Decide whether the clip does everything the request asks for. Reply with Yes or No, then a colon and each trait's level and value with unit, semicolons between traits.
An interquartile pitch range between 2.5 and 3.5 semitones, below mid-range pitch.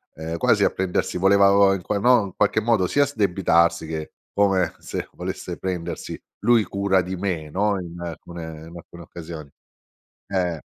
Yes: average, 2.9 semitones; very low, 95 Hz